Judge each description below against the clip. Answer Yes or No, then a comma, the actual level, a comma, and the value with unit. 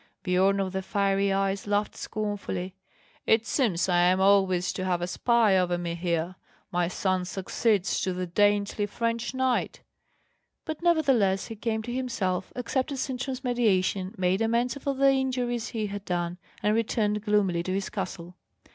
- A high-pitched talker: Yes, high, 200 Hz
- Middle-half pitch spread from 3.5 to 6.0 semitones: Yes, average, 4.0 semitones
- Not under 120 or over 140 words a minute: No, average, 160 wpm